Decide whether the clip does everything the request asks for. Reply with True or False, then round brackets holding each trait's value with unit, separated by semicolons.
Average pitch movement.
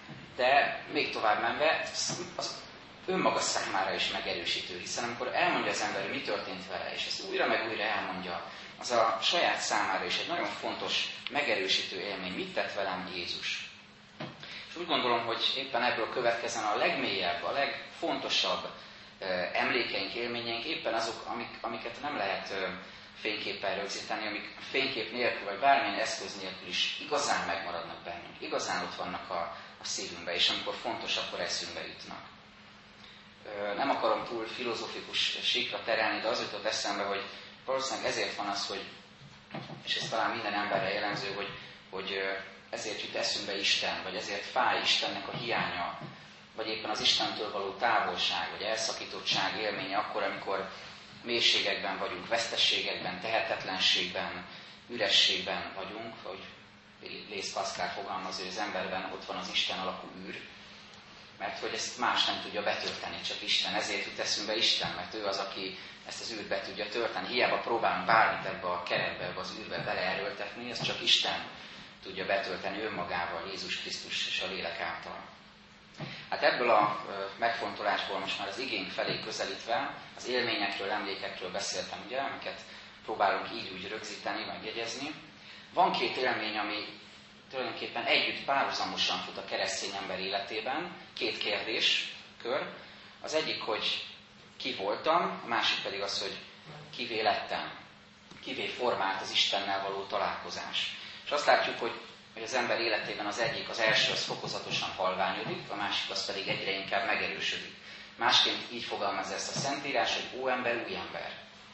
True (3.2 semitones)